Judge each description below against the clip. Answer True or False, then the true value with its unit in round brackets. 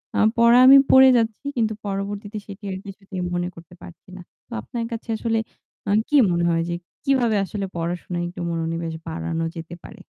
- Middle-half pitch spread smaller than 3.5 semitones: False (4.8 semitones)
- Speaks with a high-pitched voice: True (195 Hz)